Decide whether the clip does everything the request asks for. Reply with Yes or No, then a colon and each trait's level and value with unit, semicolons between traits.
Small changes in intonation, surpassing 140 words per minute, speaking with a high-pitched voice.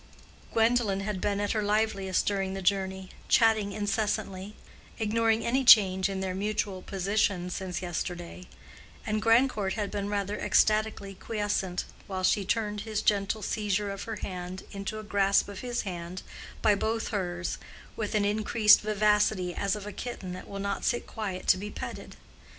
Yes: narrow, 2.0 semitones; average, 160 wpm; high, 205 Hz